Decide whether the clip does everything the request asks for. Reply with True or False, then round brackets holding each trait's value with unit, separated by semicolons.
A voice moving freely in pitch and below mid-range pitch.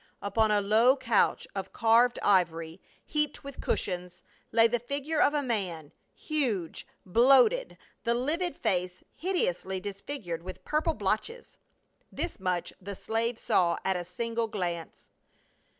False (6.1 semitones; 220 Hz)